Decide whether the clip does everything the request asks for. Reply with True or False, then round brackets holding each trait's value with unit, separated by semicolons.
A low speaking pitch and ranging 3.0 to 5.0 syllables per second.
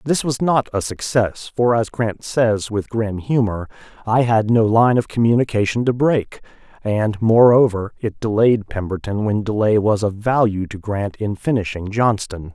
True (110 Hz; 4.5 syllables/s)